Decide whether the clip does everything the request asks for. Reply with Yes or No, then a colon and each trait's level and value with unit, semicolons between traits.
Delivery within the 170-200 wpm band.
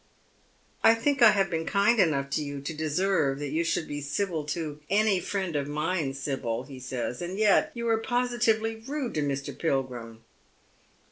Yes: average, 185 wpm